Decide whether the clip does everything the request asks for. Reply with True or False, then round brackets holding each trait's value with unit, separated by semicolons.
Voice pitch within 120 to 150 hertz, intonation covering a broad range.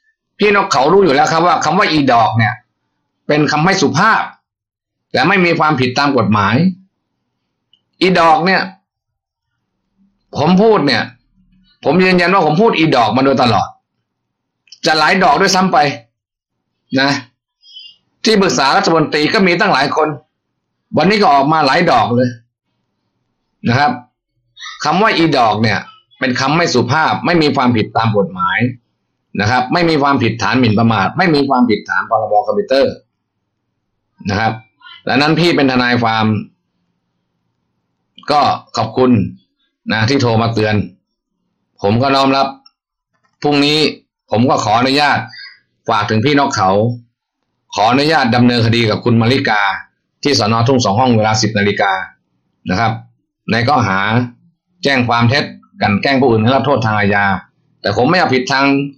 True (135 Hz; 6.0 semitones)